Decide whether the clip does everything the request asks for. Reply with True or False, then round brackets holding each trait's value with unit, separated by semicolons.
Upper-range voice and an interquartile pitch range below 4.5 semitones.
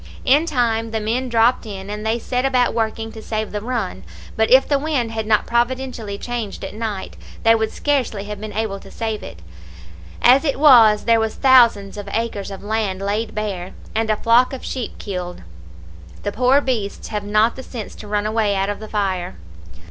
True (220 Hz; 2.8 semitones)